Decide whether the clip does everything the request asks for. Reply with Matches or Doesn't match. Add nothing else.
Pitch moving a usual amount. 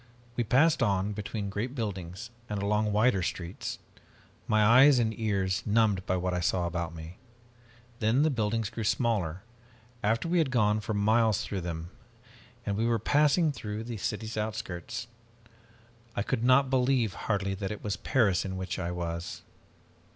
Matches